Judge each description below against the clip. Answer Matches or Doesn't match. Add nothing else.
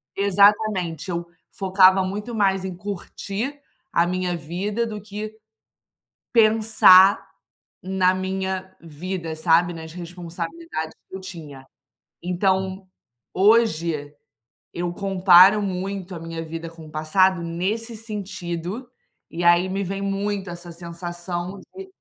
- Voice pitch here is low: Doesn't match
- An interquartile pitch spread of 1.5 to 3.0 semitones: Matches